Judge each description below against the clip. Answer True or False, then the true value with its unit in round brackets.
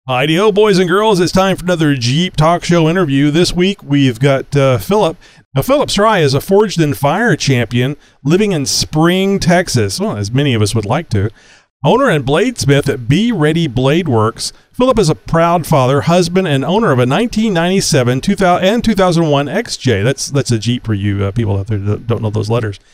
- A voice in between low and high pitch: True (145 Hz)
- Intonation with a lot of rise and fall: True (6.4 semitones)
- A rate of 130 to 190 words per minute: False (205 wpm)